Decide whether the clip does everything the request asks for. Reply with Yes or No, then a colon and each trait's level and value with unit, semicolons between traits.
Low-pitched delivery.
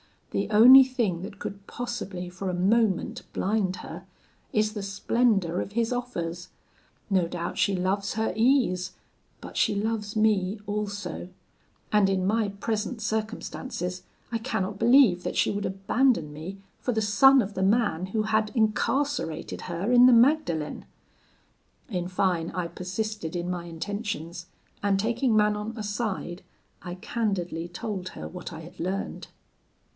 No: high, 200 Hz